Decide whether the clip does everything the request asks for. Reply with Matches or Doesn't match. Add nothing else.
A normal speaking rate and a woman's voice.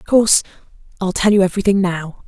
Matches